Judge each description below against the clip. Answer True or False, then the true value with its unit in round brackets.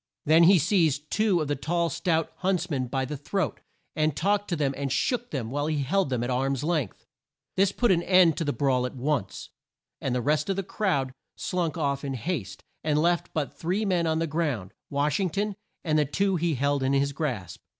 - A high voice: False (155 Hz)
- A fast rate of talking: True (220 wpm)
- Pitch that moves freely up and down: False (4.3 semitones)